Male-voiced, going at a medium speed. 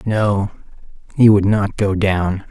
Yes: male; average, 145 wpm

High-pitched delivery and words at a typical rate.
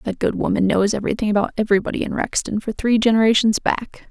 Yes: high, 215 Hz; average, 190 wpm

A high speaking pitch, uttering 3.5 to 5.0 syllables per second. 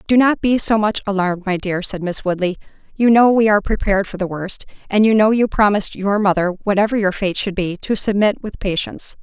No: high, 200 Hz; 5.9 syllables/s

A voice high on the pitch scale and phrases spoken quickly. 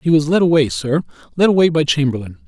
No: medium, 150 Hz; fast, 220 wpm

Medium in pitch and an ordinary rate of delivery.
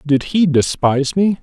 Yes: medium, 155 Hz; average, 170 wpm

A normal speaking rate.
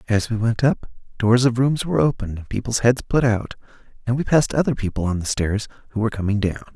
No: fast, 230 wpm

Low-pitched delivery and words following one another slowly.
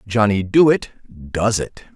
Yes: low, 105 Hz; slow, 125 wpm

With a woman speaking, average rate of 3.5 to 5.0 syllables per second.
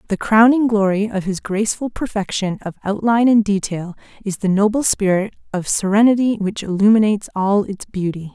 No: female; 5.3 syllables/s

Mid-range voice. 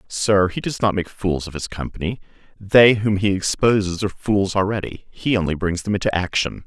No: low, 100 Hz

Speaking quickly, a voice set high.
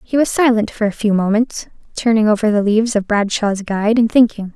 Yes: fast, 210 wpm; high, 215 Hz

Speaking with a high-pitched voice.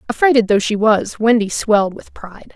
Yes: high, 220 Hz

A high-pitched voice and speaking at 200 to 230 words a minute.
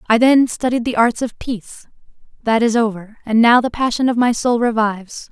Yes: high, 230 Hz; fast, 205 wpm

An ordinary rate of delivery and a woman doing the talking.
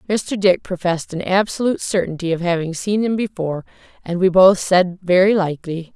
Yes: average, 170 wpm; female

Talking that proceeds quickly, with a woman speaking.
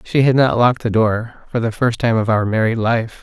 No: fast, 240 wpm; male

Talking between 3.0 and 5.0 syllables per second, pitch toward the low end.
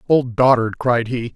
Yes: 4.3 syllables/s; low, 120 Hz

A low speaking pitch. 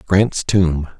Yes: very low, 90 Hz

